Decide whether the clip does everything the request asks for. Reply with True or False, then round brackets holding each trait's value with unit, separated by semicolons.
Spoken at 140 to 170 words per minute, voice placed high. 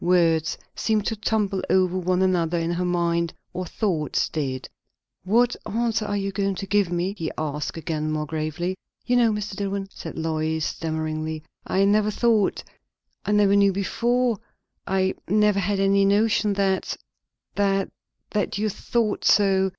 True (155 wpm; 195 Hz)